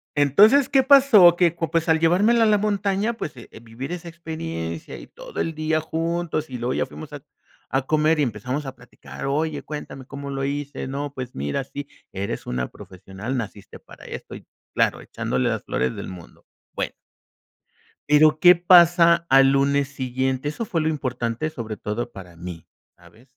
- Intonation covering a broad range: Yes, wide, 5.7 semitones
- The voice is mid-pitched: Yes, medium, 145 Hz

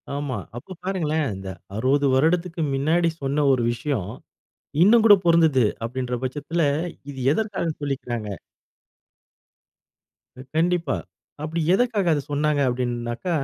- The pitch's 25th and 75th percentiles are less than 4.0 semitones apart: No, average, 4.7 semitones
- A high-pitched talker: No, medium, 145 Hz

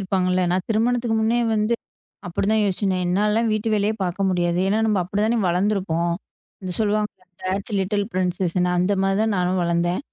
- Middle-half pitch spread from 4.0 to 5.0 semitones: No, average, 2.8 semitones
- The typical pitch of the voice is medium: No, high, 195 Hz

